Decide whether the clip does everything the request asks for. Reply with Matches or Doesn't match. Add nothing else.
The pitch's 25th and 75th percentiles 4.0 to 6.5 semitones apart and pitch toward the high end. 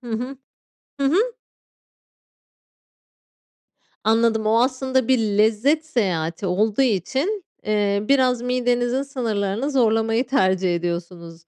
Matches